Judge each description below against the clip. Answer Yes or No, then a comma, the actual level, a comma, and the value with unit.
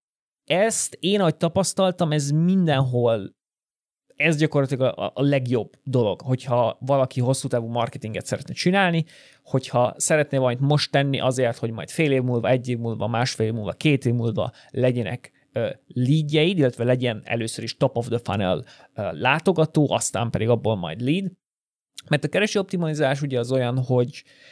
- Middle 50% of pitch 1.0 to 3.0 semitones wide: No, average, 4.1 semitones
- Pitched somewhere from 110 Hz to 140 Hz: Yes, low, 130 Hz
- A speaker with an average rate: Yes, average, 145 wpm